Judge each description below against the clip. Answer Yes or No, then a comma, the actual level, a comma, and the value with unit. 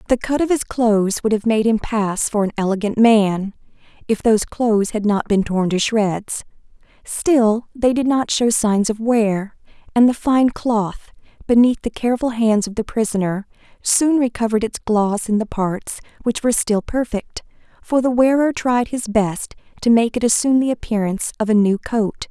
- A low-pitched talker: No, high, 225 Hz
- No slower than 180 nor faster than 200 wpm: Yes, average, 185 wpm